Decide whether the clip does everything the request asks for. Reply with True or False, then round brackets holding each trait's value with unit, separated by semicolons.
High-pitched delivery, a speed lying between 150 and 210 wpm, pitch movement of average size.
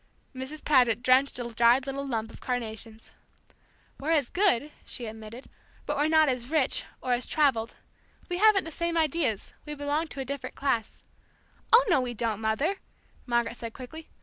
True (260 Hz; 175 wpm; 4.6 semitones)